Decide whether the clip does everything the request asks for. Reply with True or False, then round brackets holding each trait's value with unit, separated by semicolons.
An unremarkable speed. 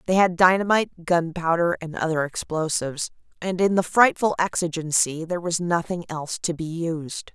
True (155 wpm)